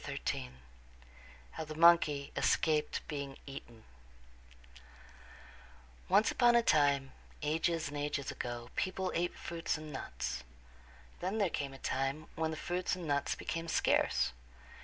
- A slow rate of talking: Yes, slow, 130 wpm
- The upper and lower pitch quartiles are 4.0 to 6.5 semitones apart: No, average, 3.5 semitones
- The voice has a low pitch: No, medium, 155 Hz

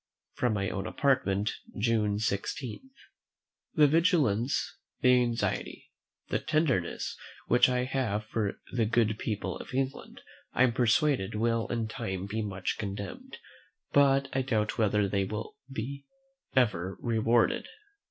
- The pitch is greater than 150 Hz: No, low, 115 Hz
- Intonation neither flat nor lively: Yes, average, 3.9 semitones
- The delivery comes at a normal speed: No, slow, 130 wpm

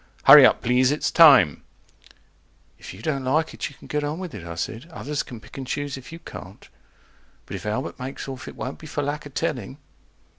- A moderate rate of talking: No, fast, 220 wpm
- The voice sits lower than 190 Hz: Yes, low, 135 Hz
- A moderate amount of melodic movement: Yes, average, 3.1 semitones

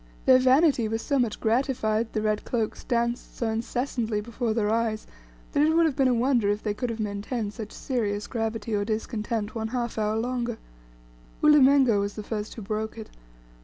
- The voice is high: Yes, high, 225 Hz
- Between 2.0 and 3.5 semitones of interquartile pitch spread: Yes, narrow, 2.6 semitones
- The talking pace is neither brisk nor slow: Yes, average, 190 wpm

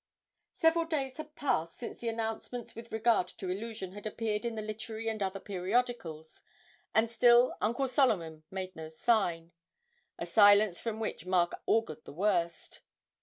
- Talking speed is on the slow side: No, average, 155 wpm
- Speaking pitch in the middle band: No, high, 215 Hz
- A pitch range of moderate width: Yes, average, 4.3 semitones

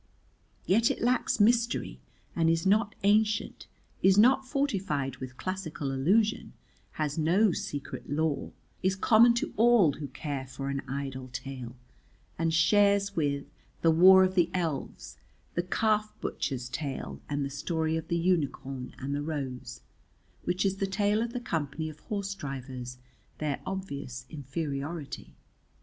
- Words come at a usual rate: Yes, average, 145 wpm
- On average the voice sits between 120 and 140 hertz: No, medium, 165 Hz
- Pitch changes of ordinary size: No, wide, 6.4 semitones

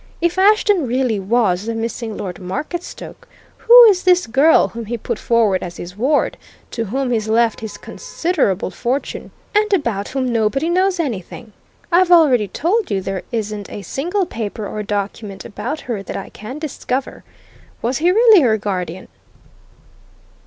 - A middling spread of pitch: No, wide, 7.9 semitones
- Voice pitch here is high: Yes, high, 235 Hz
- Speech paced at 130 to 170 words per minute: Yes, average, 160 wpm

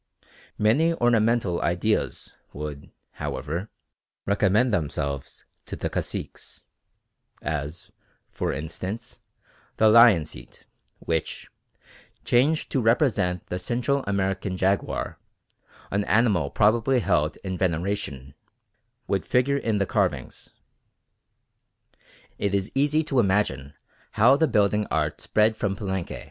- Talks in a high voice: No, low, 100 Hz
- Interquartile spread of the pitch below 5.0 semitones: No, average, 5.3 semitones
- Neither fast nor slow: No, slow, 105 wpm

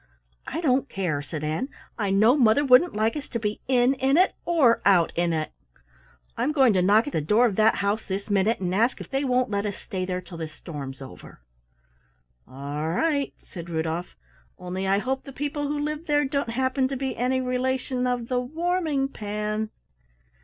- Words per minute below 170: No, average, 195 wpm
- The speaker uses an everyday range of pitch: No, wide, 6.2 semitones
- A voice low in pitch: No, high, 230 Hz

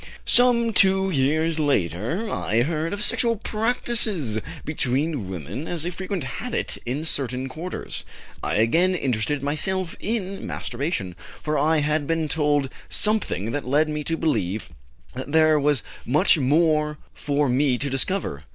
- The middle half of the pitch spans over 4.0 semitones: Yes, average, 5.2 semitones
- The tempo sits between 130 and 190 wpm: Yes, average, 140 wpm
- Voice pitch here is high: No, medium, 150 Hz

